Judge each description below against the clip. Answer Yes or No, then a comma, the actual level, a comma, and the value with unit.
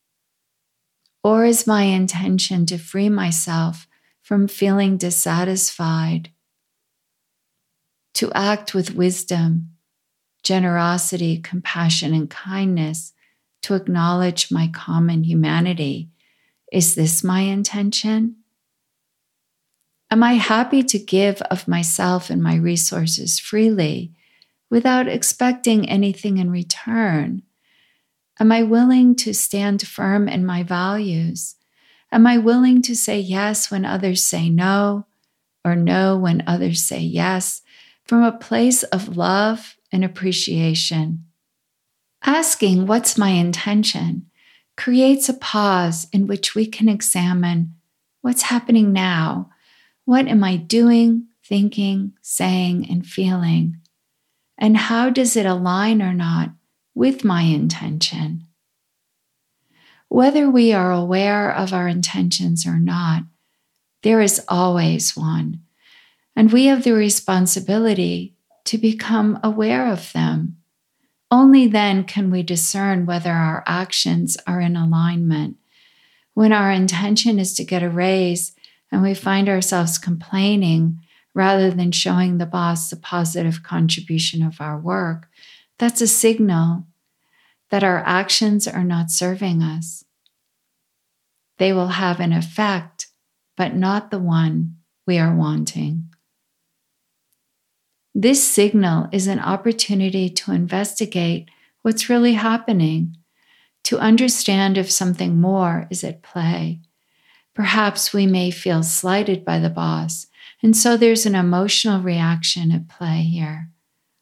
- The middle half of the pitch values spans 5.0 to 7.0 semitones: No, average, 4.1 semitones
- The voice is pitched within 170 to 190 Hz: Yes, medium, 185 Hz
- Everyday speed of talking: No, slow, 115 wpm